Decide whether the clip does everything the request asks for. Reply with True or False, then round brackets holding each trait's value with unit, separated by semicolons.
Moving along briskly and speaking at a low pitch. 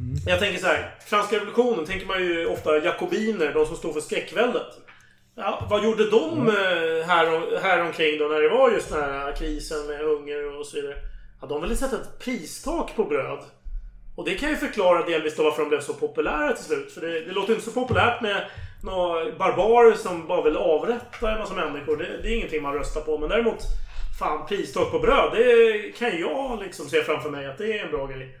False (215 wpm; 220 Hz)